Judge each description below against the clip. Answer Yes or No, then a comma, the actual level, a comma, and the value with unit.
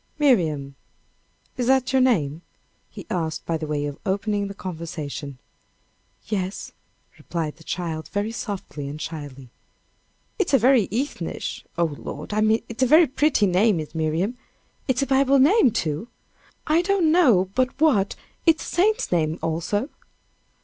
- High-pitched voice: Yes, high, 200 Hz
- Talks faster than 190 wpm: No, average, 150 wpm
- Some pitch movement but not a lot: No, wide, 8.6 semitones